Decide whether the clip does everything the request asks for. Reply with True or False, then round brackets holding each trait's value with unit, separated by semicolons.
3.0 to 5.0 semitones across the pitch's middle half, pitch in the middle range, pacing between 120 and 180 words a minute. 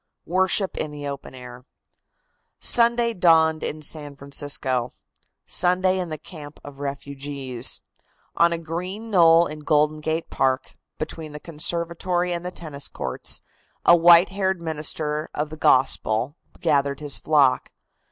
True (3.4 semitones; 155 Hz; 140 wpm)